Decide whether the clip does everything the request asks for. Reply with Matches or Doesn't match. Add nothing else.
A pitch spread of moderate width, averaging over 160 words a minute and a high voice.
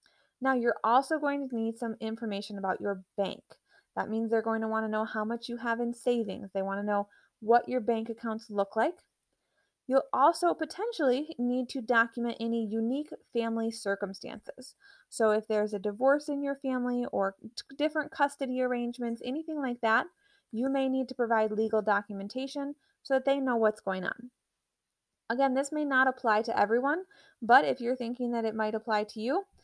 Matches